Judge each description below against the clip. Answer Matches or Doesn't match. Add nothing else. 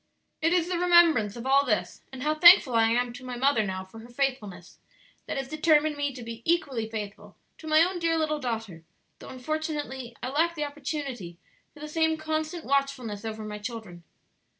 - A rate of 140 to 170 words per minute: Doesn't match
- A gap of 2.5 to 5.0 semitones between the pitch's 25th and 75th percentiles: Doesn't match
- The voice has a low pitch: Doesn't match